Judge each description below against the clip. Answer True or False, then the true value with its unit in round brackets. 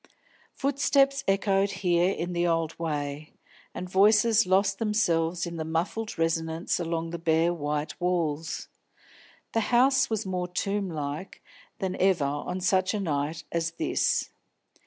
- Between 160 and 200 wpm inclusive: False (135 wpm)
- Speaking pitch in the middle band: True (175 Hz)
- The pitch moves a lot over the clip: False (3.3 semitones)